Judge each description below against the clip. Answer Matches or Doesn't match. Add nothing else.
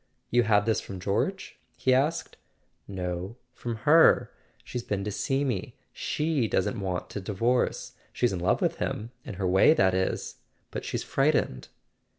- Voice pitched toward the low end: Matches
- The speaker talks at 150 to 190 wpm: Matches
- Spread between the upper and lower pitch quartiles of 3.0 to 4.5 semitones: Doesn't match